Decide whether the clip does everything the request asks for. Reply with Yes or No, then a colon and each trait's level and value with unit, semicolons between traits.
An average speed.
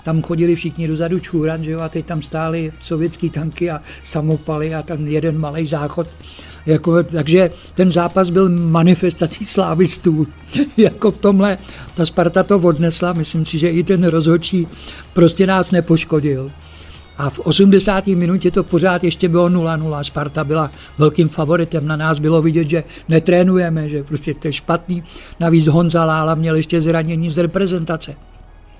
Yes: average, 155 wpm